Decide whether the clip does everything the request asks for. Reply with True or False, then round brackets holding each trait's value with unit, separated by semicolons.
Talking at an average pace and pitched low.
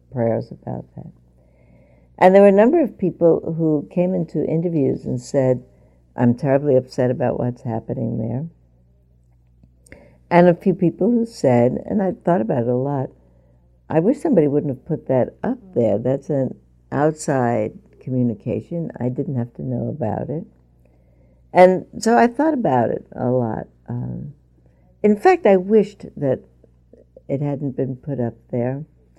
True (155 wpm; 130 Hz)